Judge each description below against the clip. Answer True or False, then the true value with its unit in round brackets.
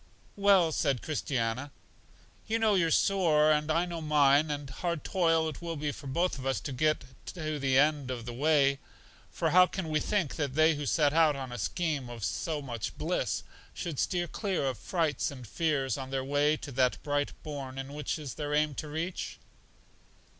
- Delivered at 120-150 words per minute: False (195 wpm)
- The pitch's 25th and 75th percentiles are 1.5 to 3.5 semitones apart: True (3.1 semitones)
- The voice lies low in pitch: False (150 Hz)